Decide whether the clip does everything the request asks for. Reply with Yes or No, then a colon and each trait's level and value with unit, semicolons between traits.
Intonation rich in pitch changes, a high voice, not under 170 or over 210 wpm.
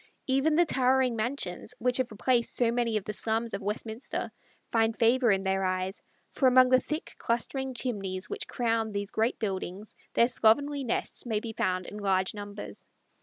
No: average, 3.8 semitones; high, 230 Hz; average, 175 wpm